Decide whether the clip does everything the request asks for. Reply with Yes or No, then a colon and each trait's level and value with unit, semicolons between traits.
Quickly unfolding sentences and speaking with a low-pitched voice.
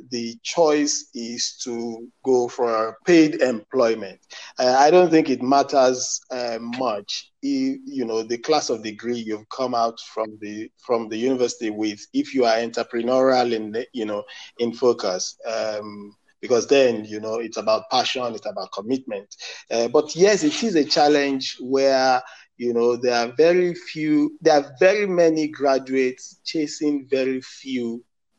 No: average, 155 wpm; low, 125 Hz